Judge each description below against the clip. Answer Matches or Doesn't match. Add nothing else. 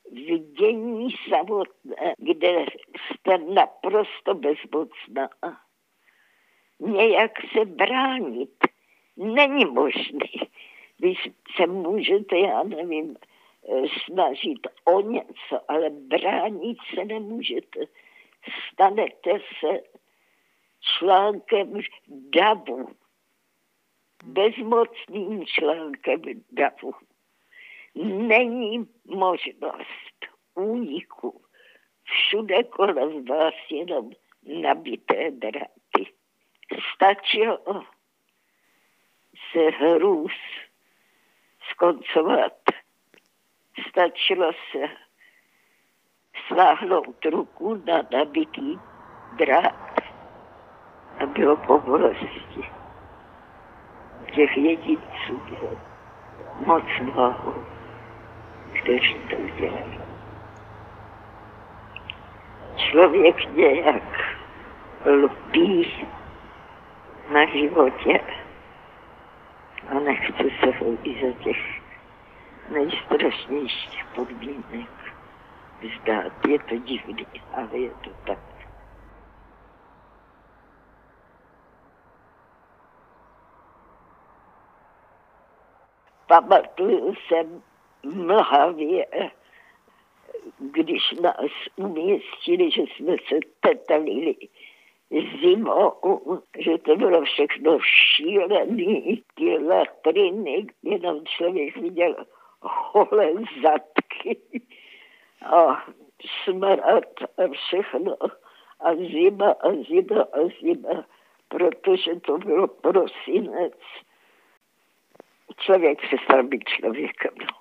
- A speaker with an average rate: Doesn't match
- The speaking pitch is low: Doesn't match